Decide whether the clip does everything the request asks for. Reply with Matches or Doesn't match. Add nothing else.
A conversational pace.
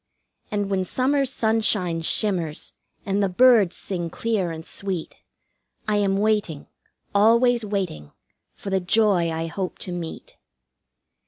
Doesn't match